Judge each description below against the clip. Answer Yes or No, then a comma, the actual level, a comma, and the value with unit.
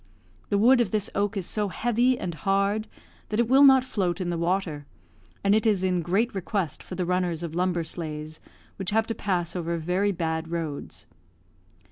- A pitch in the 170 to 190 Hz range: Yes, medium, 185 Hz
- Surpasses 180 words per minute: Yes, average, 190 wpm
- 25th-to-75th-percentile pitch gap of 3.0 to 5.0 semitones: Yes, average, 3.8 semitones